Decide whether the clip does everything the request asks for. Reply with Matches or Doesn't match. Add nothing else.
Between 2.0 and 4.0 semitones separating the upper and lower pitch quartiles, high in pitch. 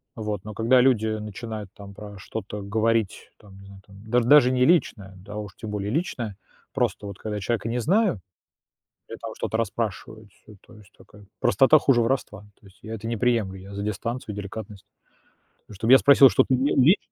Doesn't match